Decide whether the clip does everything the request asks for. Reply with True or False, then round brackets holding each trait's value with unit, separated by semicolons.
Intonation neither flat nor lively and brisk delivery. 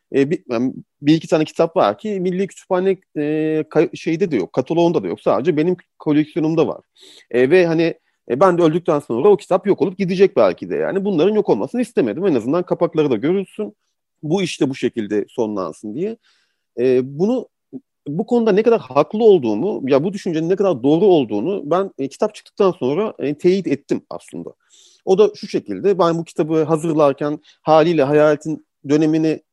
True (4.4 semitones; 180 wpm)